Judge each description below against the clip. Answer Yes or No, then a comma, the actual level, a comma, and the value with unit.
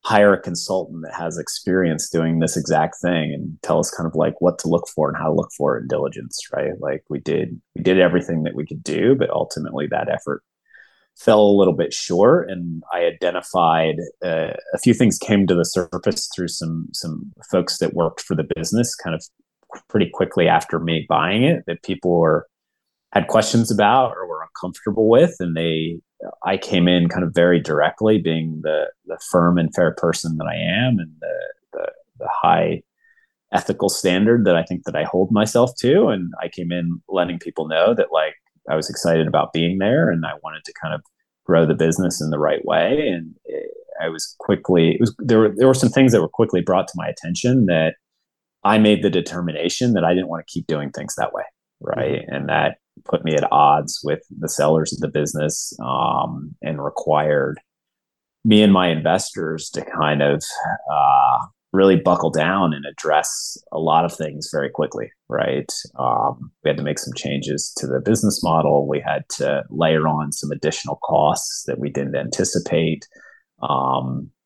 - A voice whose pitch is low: Yes, very low, 85 Hz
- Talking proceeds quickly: No, average, 195 wpm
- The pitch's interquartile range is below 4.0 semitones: No, average, 4.6 semitones